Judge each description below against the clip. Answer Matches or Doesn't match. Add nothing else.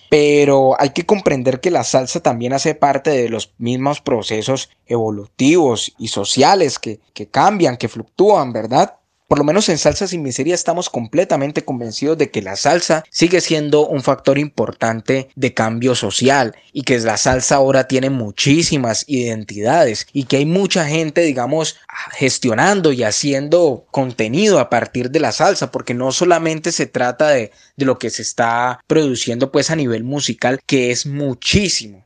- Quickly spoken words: Doesn't match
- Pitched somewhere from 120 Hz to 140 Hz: Matches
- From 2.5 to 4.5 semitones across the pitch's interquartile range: Matches